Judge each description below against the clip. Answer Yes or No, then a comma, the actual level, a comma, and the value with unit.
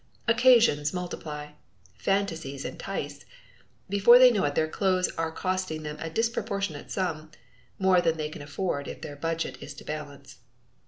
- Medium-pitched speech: Yes, medium, 165 Hz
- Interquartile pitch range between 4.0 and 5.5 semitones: Yes, average, 4.4 semitones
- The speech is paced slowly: No, average, 150 wpm